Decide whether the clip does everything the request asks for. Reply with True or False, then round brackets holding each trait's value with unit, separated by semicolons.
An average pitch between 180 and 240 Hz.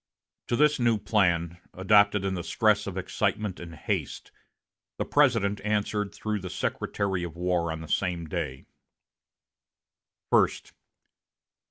False (100 Hz)